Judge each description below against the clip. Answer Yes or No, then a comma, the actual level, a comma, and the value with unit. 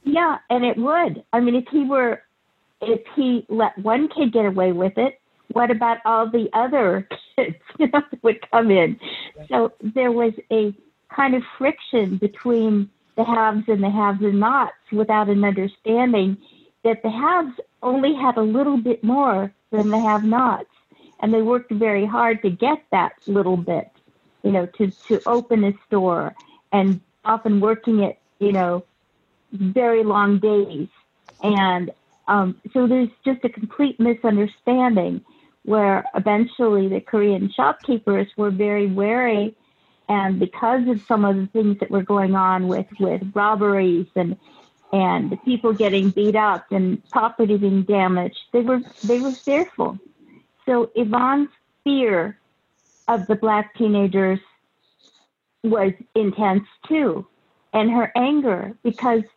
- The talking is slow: No, average, 150 wpm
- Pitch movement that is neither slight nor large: Yes, average, 3.3 semitones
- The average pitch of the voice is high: Yes, high, 220 Hz